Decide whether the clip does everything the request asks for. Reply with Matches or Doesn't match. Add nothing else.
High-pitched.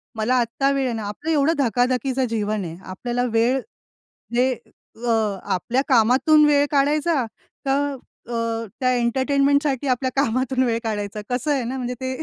Matches